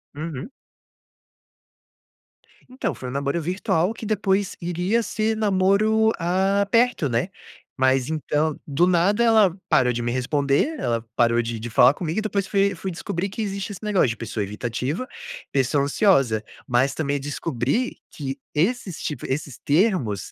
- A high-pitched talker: No, medium, 165 Hz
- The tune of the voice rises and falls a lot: Yes, wide, 7.1 semitones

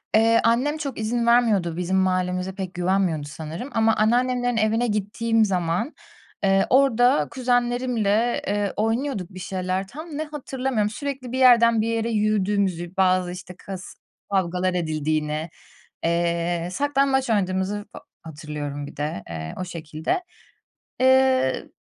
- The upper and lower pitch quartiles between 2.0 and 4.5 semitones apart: No, average, 5.3 semitones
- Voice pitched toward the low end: No, high, 205 Hz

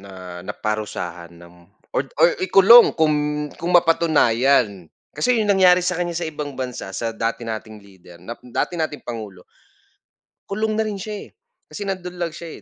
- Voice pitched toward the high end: No, medium, 150 Hz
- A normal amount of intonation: No, wide, 8.7 semitones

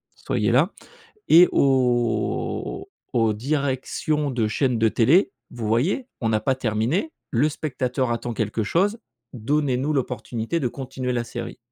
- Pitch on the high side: No, low, 125 Hz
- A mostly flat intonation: No, average, 4.0 semitones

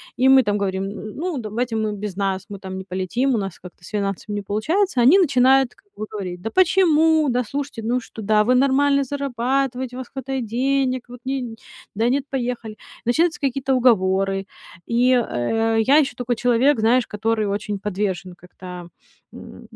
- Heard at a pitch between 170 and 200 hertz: No, high, 235 Hz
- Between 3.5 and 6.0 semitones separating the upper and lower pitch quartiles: Yes, average, 4.5 semitones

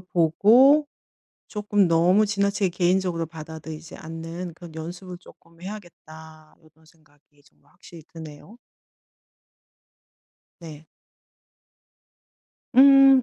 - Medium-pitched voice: Yes, medium, 170 Hz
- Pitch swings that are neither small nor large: Yes, average, 3.9 semitones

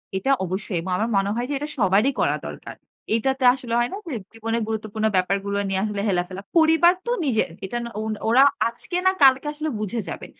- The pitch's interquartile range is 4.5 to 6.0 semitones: Yes, average, 5.1 semitones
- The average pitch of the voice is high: Yes, high, 225 Hz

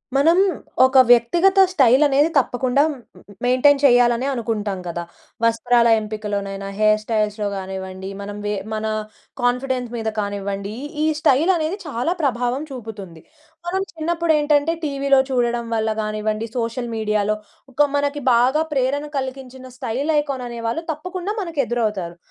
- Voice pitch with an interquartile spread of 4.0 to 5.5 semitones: Yes, average, 4.9 semitones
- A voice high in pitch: Yes, high, 245 Hz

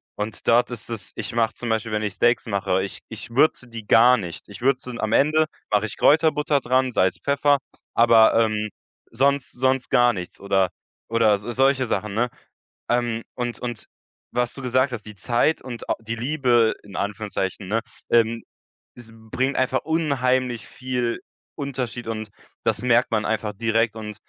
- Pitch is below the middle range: Yes, low, 115 Hz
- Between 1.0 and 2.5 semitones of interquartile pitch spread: No, average, 2.9 semitones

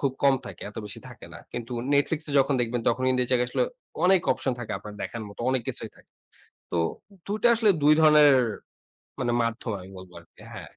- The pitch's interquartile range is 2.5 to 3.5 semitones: No, average, 4.0 semitones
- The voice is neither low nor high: No, low, 125 Hz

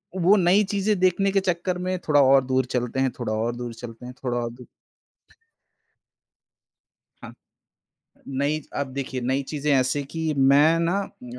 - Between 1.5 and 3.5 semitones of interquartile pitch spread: No, wide, 5.5 semitones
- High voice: No, medium, 140 Hz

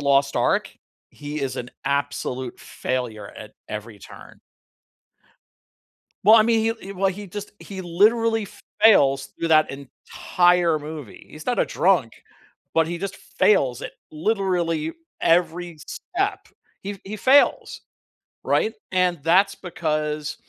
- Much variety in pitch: Yes, wide, 5.7 semitones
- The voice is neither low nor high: Yes, medium, 170 Hz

